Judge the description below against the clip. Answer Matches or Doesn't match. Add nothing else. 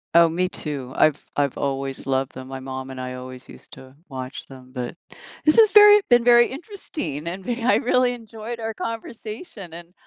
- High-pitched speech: Doesn't match